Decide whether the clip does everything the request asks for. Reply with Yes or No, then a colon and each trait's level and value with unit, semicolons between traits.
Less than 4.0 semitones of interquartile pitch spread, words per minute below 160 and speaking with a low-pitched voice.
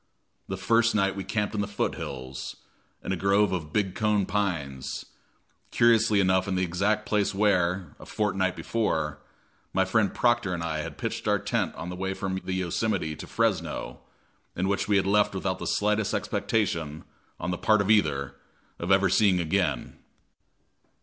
No: average, 2.9 semitones; average, 175 wpm; very low, 95 Hz